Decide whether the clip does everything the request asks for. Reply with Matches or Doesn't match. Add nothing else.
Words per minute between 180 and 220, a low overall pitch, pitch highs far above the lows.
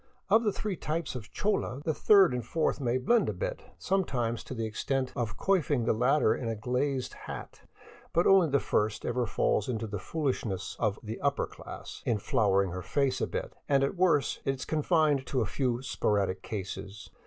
Matches